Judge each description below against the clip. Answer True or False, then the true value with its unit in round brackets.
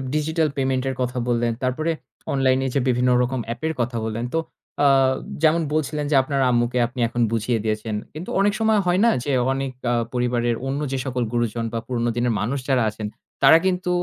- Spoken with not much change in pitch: False (3.5 semitones)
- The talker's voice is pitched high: False (130 Hz)